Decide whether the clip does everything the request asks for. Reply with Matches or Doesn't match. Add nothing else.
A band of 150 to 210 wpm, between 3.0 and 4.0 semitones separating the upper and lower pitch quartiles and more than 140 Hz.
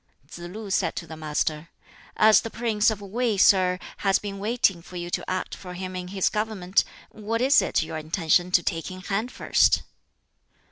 Matches